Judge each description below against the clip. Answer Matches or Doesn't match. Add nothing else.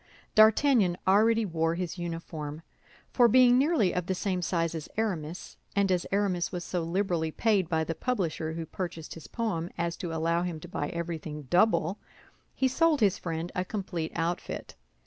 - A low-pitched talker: Doesn't match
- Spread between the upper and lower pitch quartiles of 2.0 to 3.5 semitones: Doesn't match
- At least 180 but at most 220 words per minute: Doesn't match